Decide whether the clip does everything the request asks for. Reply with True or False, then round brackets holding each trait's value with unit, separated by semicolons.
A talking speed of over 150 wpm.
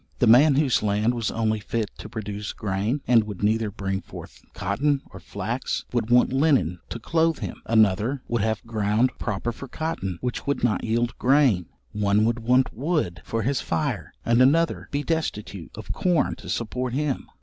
True (180 wpm)